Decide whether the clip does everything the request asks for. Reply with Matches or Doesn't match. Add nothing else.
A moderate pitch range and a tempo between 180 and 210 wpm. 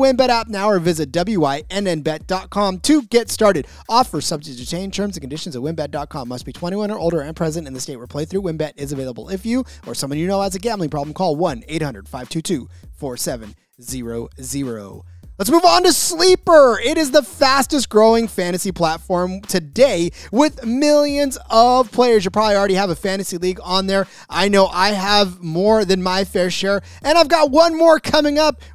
Doesn't match